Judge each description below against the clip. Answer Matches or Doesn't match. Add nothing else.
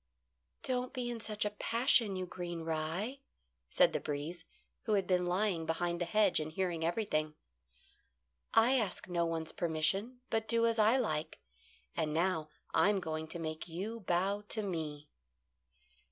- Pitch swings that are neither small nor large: Matches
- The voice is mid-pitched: Matches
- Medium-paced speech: Matches